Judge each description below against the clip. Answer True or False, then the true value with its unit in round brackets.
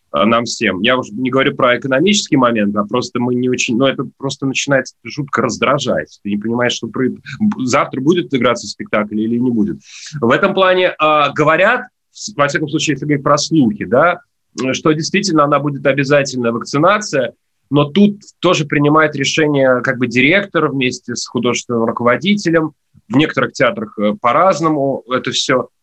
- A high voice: False (135 Hz)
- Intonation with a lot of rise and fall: False (4.3 semitones)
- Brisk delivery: True (165 wpm)